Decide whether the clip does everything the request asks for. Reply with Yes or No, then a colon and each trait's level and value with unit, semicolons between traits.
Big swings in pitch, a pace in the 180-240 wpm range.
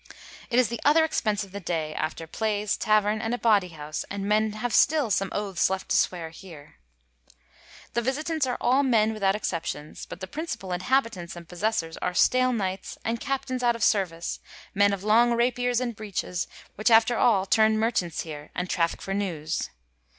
No: average, 4.7 semitones; average, 185 wpm